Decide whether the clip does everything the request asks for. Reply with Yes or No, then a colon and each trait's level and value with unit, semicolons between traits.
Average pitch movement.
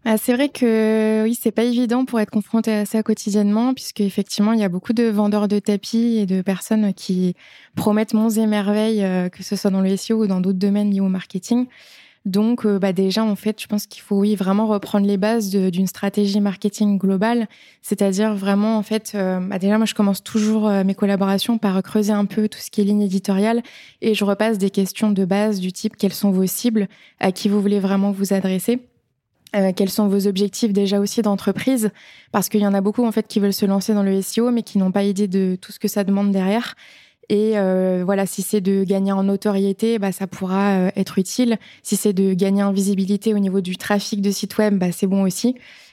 No: narrow, 1.8 semitones